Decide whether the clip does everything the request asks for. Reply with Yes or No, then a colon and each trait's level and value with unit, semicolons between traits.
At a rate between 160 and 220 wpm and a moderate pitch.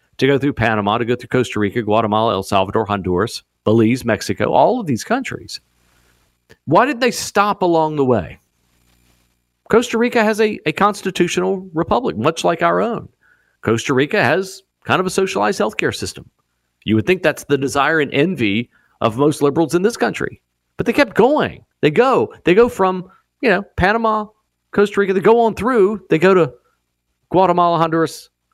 Yes: average, 175 wpm; medium, 150 Hz